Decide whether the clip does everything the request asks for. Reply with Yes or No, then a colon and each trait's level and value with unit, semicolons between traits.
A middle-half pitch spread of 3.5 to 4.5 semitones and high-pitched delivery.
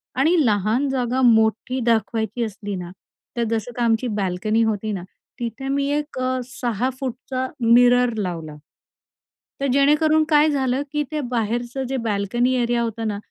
No: average, 3.1 semitones; high, 240 Hz